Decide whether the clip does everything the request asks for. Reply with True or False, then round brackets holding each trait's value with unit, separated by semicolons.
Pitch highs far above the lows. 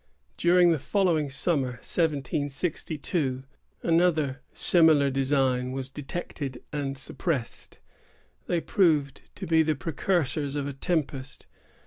False (3.6 semitones)